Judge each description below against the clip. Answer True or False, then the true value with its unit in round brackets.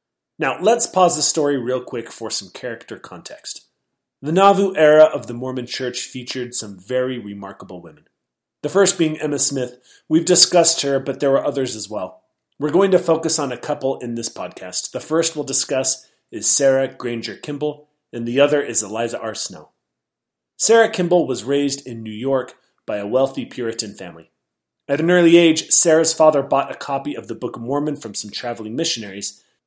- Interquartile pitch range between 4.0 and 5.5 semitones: True (4.4 semitones)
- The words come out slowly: False (185 wpm)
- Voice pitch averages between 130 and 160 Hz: True (135 Hz)